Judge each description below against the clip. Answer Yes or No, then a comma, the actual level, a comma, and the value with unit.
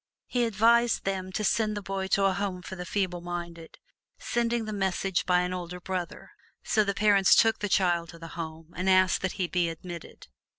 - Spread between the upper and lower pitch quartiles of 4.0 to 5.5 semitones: No, narrow, 2.5 semitones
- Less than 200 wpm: No, fast, 205 wpm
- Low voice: No, medium, 185 Hz